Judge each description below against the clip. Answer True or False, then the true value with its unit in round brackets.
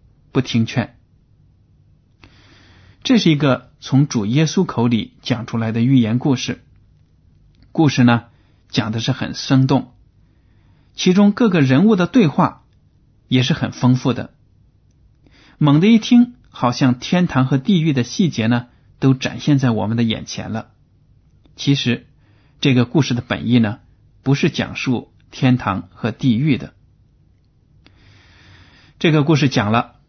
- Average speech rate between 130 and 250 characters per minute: True (190 characters per minute)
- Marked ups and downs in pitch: False (4.2 semitones)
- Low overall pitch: True (125 Hz)